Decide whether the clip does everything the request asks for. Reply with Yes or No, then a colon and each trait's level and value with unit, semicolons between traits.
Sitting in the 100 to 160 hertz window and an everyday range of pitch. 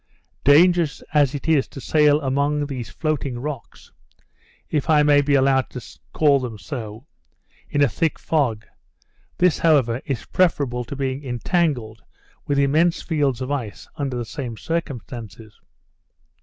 Yes: medium, 140 Hz; average, 3.5 semitones